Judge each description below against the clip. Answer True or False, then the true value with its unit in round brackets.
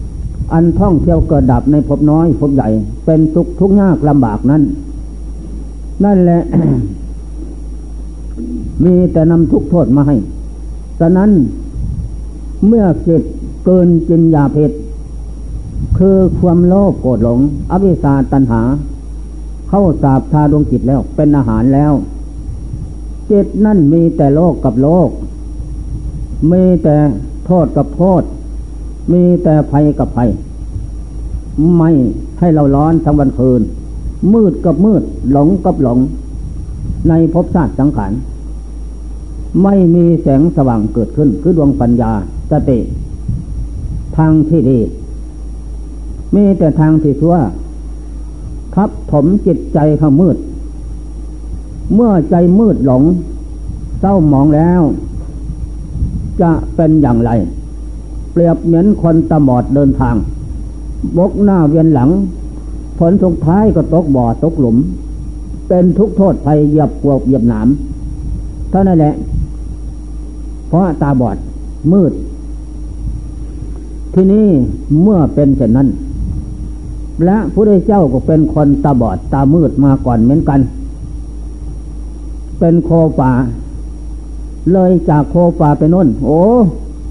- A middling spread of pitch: False (6.0 semitones)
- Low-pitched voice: False (150 Hz)